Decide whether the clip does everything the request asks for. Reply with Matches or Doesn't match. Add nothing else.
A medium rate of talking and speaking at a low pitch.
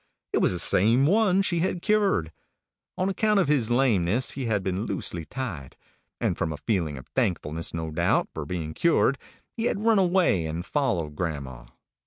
Matches